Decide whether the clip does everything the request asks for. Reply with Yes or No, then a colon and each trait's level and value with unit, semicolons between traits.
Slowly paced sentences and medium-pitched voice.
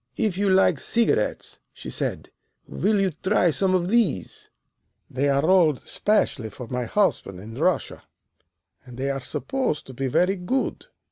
No: average, 155 wpm; medium, 175 Hz